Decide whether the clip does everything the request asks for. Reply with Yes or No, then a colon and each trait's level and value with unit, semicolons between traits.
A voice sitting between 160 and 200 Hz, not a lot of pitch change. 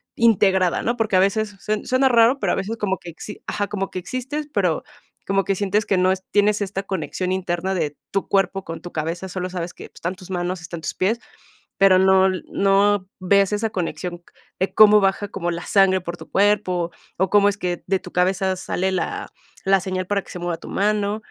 Yes: high, 190 Hz; narrow, 2.1 semitones